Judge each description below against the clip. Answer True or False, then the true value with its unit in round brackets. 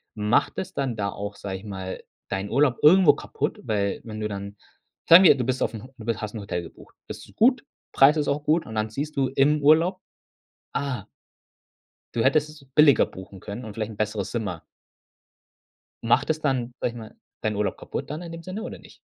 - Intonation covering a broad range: True (6.2 semitones)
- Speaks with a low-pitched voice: True (120 Hz)